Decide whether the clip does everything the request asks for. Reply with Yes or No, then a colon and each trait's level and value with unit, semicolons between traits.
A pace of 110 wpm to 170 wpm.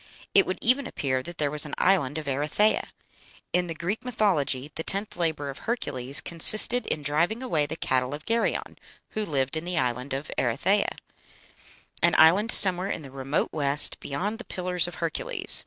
No: average, 180 wpm